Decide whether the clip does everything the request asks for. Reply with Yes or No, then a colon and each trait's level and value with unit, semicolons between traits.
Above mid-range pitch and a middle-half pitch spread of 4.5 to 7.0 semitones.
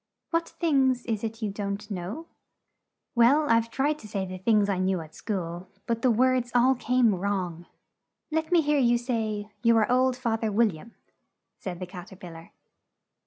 Yes: high, 225 Hz; average, 4.8 semitones